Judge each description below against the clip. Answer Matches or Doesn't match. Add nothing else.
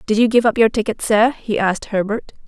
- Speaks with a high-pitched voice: Matches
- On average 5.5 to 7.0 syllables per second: Matches